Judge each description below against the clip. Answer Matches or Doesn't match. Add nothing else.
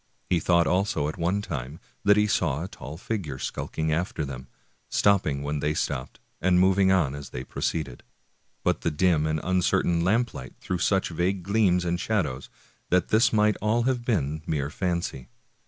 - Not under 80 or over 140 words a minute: Doesn't match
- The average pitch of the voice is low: Matches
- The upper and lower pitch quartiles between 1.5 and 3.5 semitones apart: Doesn't match